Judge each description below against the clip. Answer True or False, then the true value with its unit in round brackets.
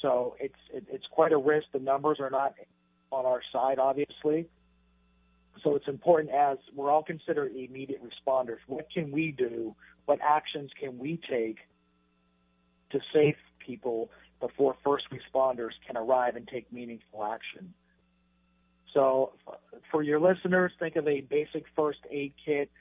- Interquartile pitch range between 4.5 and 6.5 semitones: True (5.3 semitones)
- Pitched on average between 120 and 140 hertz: True (135 Hz)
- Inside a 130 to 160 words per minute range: True (145 wpm)